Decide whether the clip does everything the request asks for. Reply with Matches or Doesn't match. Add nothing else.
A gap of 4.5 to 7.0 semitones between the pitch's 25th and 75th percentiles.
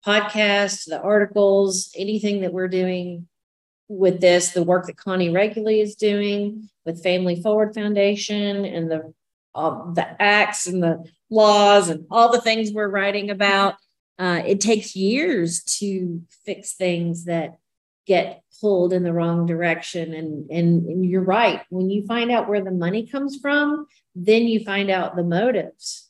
Doesn't match